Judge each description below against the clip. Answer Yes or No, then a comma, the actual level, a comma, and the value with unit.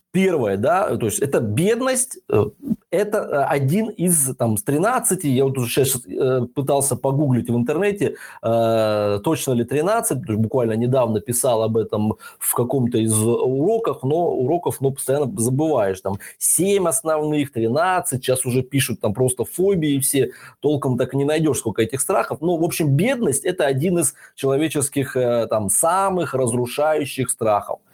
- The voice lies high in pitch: No, low, 135 Hz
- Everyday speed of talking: Yes, average, 145 wpm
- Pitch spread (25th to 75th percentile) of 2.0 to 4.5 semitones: No, average, 5.3 semitones